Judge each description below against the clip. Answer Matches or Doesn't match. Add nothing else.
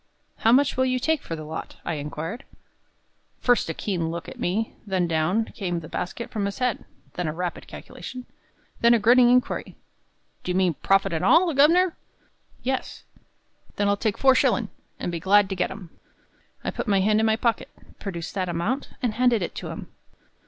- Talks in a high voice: Matches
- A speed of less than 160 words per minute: Doesn't match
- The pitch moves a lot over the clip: Matches